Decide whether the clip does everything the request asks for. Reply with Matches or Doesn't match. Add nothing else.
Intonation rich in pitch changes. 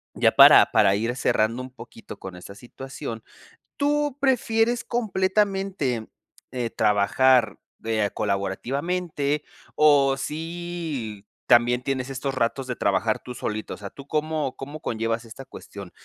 Matches